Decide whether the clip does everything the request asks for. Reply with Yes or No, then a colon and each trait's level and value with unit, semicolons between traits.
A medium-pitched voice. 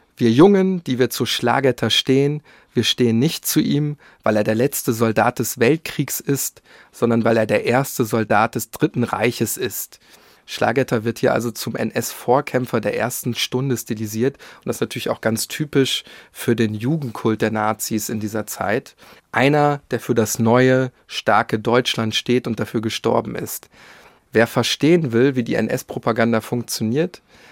No: low, 120 Hz